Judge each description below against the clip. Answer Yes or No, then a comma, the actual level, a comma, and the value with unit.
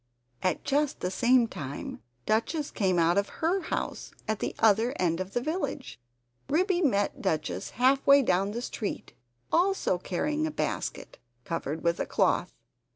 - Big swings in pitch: Yes, wide, 8.2 semitones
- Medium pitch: No, high, 225 Hz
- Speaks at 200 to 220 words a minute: No, average, 160 wpm